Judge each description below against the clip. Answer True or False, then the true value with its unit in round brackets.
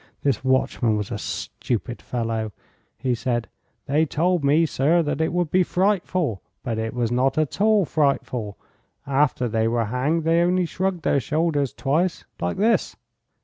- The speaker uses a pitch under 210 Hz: True (140 Hz)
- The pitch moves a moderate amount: False (5.7 semitones)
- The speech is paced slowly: False (160 wpm)